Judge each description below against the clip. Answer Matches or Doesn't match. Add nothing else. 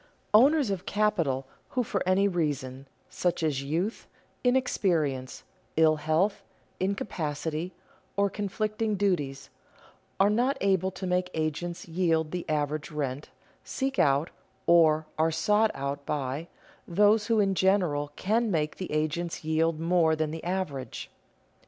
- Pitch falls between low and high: Matches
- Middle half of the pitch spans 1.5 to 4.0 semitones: Doesn't match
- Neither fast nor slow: Doesn't match